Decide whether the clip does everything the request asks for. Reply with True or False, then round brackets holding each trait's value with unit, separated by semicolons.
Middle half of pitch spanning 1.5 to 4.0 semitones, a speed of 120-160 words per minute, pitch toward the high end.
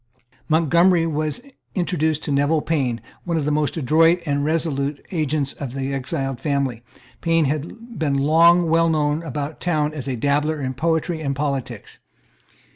False (2.8 semitones; 155 wpm; 150 Hz)